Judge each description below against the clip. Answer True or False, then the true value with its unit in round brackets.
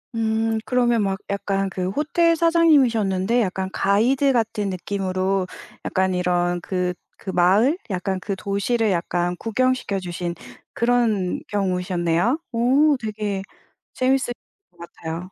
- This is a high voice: True (200 Hz)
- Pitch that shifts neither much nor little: True (4.3 semitones)